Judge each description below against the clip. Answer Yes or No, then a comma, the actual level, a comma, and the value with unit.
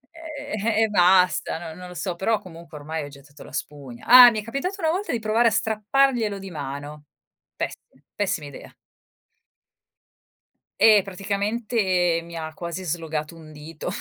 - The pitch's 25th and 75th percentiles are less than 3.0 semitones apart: No, wide, 5.7 semitones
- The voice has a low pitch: No, medium, 185 Hz